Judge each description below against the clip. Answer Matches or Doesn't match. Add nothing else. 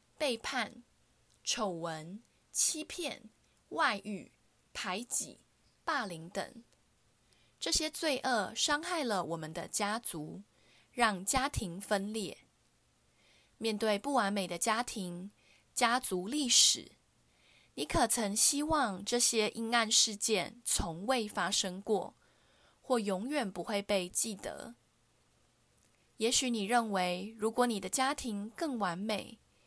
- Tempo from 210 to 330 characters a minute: Doesn't match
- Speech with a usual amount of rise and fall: Matches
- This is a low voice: Doesn't match